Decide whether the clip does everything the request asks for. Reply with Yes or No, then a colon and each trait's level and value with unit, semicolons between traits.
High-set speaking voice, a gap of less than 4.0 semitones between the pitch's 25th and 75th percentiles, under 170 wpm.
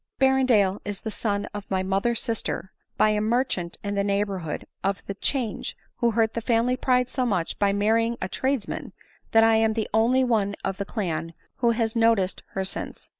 No: high, 220 Hz; average, 2.9 semitones; average, 190 wpm